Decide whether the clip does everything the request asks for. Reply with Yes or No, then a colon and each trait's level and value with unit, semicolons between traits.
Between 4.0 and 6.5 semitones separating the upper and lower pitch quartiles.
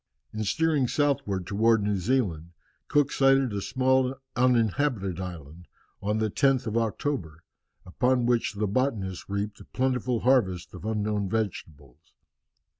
Yes: average, 5.2 semitones